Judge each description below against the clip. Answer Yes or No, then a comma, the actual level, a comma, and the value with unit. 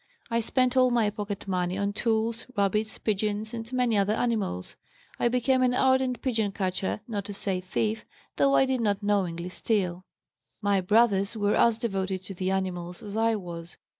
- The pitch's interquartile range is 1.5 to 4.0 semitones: Yes, average, 3.3 semitones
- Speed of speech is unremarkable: Yes, average, 175 wpm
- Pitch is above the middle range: Yes, high, 210 Hz